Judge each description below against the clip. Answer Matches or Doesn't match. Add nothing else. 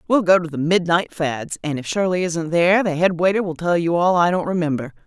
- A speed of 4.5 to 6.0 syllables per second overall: Matches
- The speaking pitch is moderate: Matches